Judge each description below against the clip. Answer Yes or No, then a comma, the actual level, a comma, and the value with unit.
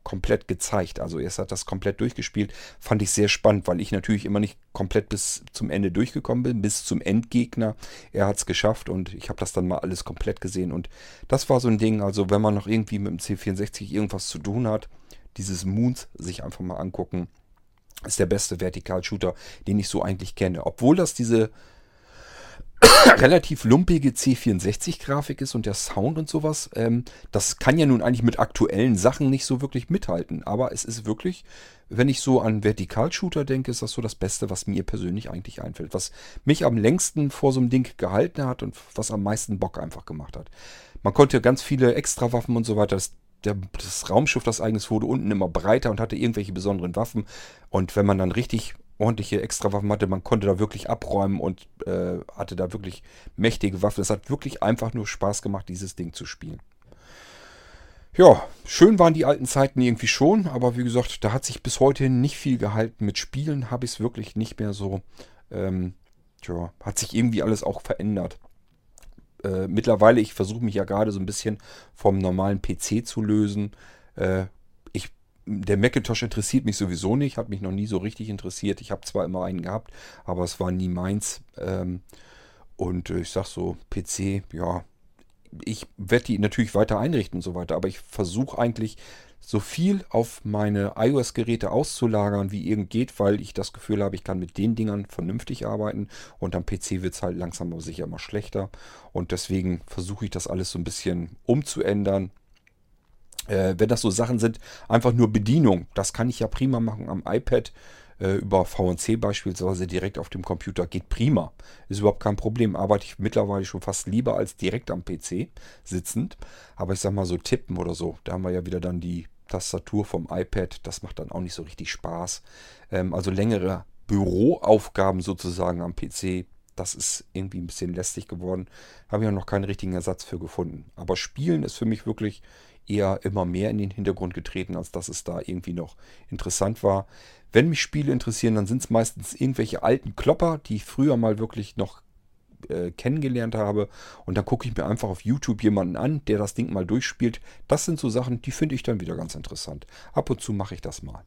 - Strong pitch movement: No, average, 3.7 semitones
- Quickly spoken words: Yes, fast, 195 wpm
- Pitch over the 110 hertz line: No, low, 105 Hz